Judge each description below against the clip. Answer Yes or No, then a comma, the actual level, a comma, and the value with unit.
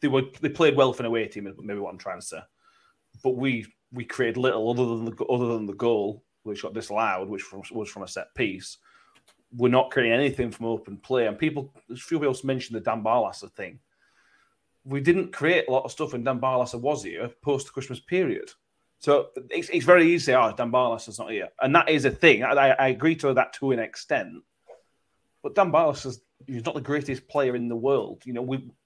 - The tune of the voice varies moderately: Yes, average, 3.0 semitones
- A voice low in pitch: Yes, low, 130 Hz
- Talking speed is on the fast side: Yes, fast, 225 wpm